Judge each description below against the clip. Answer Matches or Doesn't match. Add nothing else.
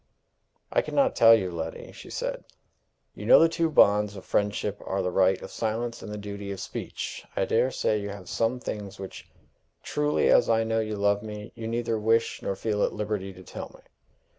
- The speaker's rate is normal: Doesn't match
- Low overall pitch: Matches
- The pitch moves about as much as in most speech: Doesn't match